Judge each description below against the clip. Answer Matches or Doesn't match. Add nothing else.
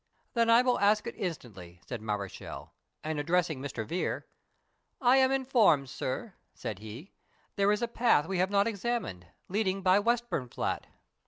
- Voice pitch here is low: Doesn't match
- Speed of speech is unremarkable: Matches